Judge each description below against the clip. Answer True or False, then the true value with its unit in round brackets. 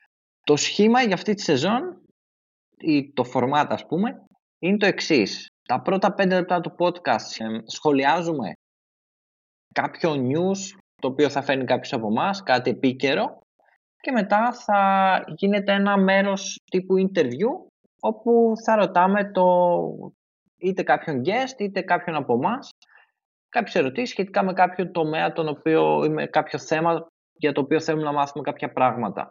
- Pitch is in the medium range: True (175 Hz)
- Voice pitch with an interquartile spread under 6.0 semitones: True (5.5 semitones)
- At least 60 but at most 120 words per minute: False (145 wpm)